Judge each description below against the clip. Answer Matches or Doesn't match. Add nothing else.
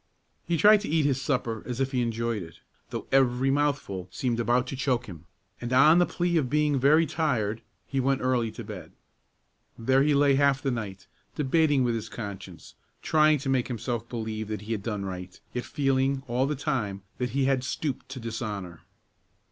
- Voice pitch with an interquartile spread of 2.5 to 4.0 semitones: Matches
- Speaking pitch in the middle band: Doesn't match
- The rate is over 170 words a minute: Matches